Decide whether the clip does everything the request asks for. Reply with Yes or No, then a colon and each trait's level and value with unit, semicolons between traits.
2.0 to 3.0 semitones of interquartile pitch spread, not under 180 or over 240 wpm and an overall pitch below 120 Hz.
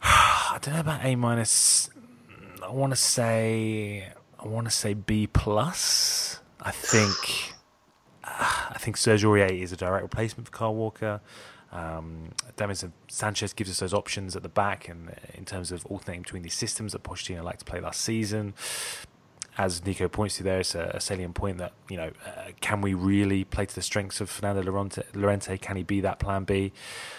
Yes: average, 2.7 semitones; average, 190 wpm; low, 100 Hz